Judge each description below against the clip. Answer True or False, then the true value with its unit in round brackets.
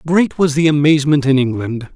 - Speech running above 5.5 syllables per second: True (5.7 syllables/s)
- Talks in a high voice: False (145 Hz)